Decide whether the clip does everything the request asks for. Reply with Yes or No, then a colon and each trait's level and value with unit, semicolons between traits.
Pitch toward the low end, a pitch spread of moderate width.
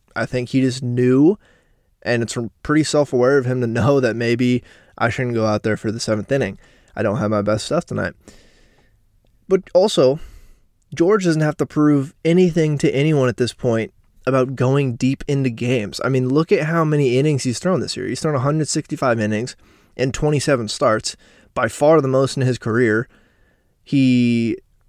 Yes: low, 125 Hz; average, 3.9 semitones